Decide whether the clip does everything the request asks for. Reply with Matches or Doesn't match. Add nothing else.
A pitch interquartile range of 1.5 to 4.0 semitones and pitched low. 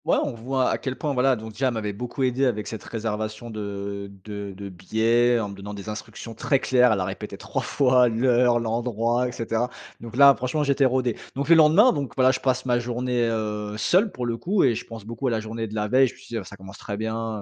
Matches